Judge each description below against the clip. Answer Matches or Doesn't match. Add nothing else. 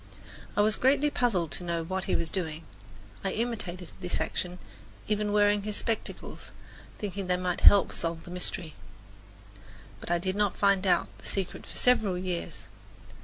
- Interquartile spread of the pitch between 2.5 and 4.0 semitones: Matches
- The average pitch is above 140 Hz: Matches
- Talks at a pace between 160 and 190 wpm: Matches